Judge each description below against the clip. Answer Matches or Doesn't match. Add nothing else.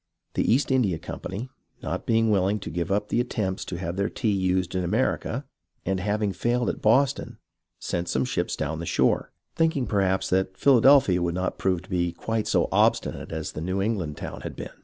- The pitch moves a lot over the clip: Doesn't match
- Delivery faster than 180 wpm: Matches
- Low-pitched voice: Matches